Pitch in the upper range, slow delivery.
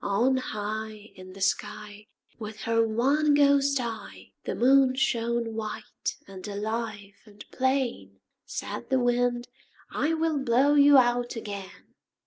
Yes: high, 235 Hz; slow, 130 wpm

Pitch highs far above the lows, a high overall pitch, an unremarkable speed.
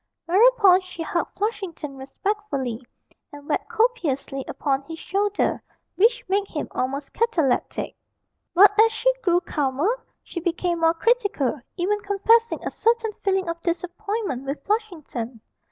No: wide, 6.2 semitones; very high, 365 Hz; slow, 130 wpm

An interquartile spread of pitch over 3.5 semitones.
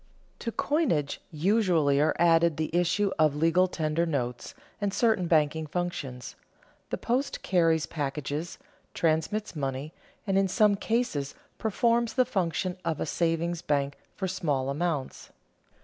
Yes: average, 4.5 semitones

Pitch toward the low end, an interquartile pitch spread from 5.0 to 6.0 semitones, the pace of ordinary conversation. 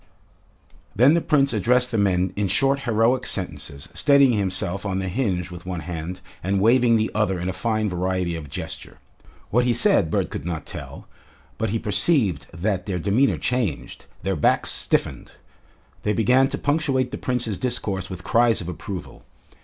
Yes: low, 105 Hz; average, 5.3 semitones; average, 170 wpm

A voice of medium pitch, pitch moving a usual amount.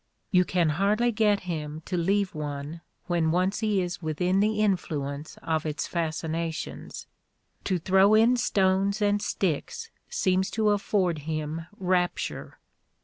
Yes: medium, 180 Hz; average, 4.1 semitones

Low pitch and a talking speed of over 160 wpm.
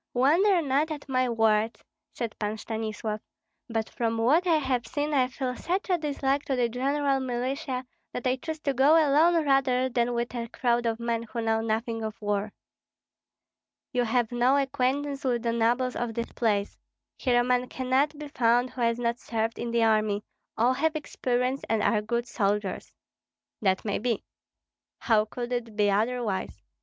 No: high, 245 Hz; average, 175 wpm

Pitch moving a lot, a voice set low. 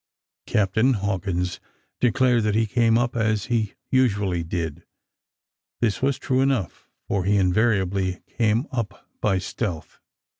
No: average, 3.9 semitones; low, 105 Hz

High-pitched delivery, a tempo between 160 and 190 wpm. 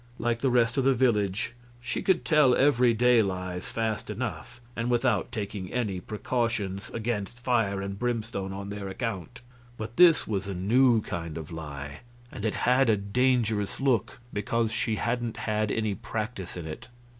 No: low, 110 Hz; average, 165 wpm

